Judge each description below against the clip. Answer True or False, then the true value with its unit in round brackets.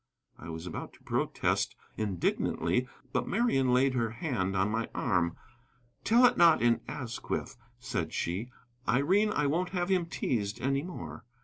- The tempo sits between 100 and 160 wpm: True (150 wpm)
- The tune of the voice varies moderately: False (8.1 semitones)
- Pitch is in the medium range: False (125 Hz)